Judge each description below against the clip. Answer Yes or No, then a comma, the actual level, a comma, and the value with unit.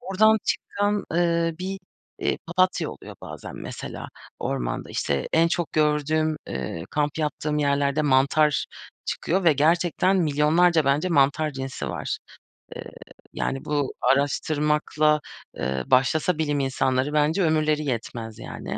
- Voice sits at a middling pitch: Yes, medium, 150 Hz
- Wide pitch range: No, average, 3.2 semitones